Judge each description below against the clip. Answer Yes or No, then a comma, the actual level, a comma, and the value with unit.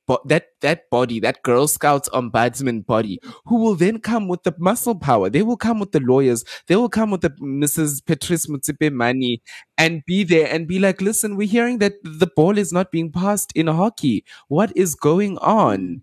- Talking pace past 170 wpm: Yes, average, 200 wpm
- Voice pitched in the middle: Yes, medium, 165 Hz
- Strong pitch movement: Yes, wide, 6.4 semitones